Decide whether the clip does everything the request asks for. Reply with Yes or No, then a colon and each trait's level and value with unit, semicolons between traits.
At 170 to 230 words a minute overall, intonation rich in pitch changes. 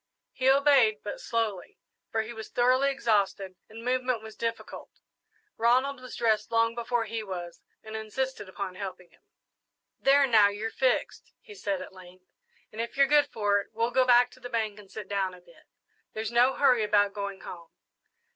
No: average, 185 wpm; average, 3.7 semitones